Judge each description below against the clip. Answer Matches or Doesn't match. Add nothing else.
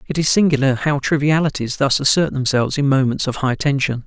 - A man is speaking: Matches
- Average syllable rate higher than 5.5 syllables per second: Matches